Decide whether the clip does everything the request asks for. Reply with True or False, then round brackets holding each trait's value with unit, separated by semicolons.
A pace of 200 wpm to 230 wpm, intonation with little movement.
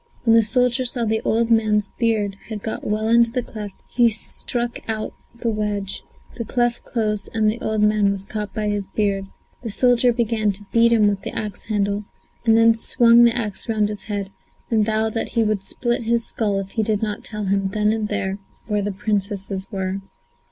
True (205 wpm; 2.1 semitones)